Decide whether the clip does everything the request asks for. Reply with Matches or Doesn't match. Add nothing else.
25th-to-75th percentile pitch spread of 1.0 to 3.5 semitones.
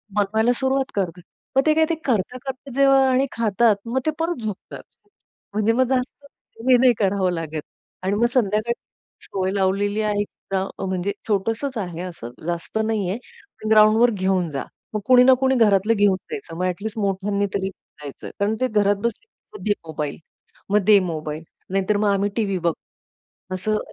Doesn't match